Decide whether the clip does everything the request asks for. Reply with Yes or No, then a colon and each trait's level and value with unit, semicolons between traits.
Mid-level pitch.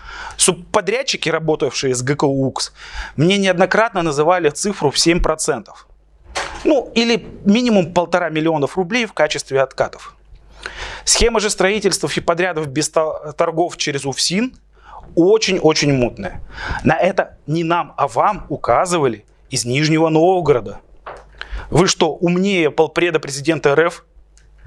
Yes: medium, 165 Hz